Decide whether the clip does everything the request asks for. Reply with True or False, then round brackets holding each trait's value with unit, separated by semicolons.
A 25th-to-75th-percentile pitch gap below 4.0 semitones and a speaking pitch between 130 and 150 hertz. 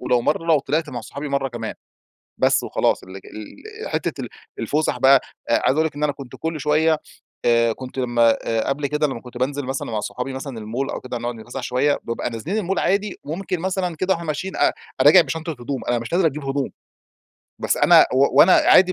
False (4.6 semitones; 140 Hz)